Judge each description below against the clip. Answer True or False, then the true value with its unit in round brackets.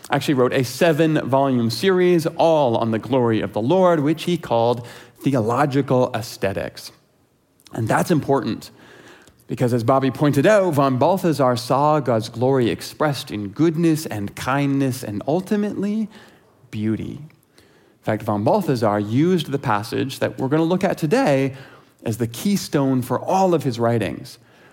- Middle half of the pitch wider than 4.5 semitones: True (5.3 semitones)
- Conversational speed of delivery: True (150 wpm)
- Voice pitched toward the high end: False (135 Hz)